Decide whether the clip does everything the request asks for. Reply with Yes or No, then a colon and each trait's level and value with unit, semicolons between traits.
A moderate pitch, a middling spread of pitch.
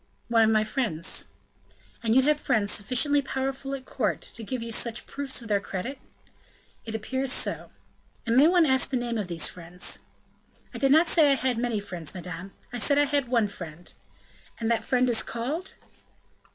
No: high, 235 Hz; average, 4.2 semitones